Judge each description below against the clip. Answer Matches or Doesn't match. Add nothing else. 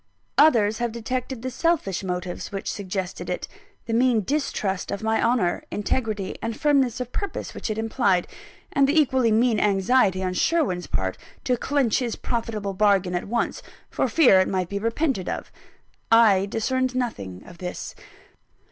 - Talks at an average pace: Matches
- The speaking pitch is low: Doesn't match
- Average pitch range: Matches